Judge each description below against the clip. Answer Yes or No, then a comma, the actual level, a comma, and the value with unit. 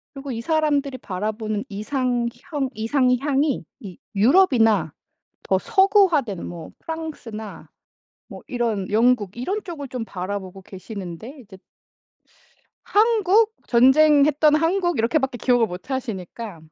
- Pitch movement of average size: No, wide, 6.1 semitones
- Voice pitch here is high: Yes, very high, 250 Hz